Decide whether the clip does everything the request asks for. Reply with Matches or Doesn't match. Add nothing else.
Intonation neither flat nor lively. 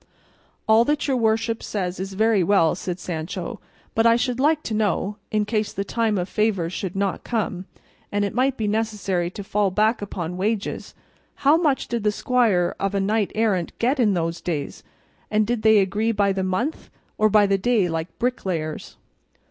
Matches